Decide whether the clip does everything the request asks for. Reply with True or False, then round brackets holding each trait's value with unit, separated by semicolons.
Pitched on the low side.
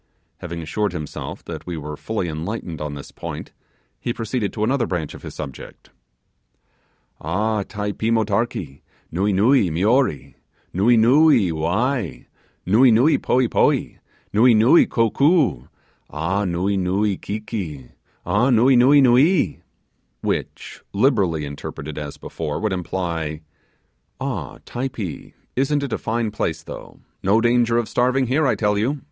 True (105 Hz)